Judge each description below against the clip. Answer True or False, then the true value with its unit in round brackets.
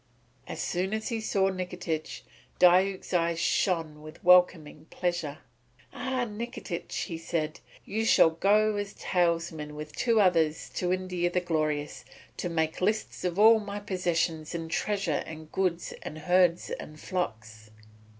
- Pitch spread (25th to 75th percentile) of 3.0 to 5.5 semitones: True (3.5 semitones)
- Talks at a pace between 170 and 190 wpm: False (140 wpm)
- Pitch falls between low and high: True (175 Hz)